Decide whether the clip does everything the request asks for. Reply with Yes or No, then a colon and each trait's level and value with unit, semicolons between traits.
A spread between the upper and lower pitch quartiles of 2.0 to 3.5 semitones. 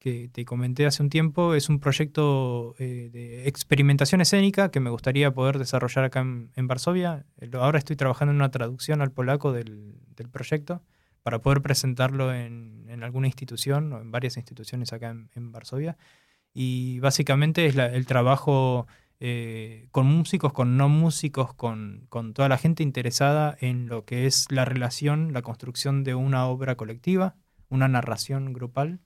Yes: average, 3.0 semitones